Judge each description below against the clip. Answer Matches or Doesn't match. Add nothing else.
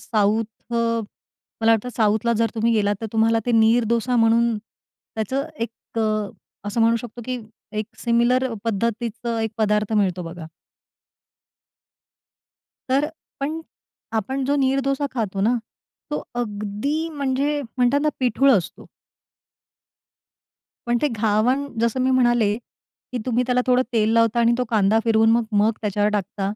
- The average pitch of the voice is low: Doesn't match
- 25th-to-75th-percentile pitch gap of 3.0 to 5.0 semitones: Doesn't match